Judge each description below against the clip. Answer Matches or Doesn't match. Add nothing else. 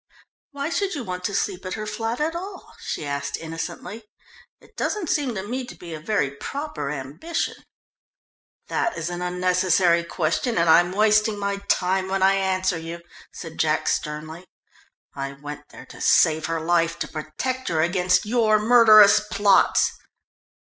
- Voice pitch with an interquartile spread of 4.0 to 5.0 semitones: Matches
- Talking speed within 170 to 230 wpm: Doesn't match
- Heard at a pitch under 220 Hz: Matches